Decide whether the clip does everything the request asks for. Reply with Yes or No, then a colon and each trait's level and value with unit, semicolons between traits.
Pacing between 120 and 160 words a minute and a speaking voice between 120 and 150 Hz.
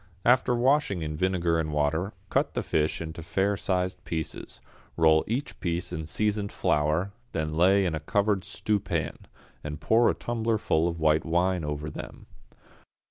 No: average, 155 wpm; very low, 85 Hz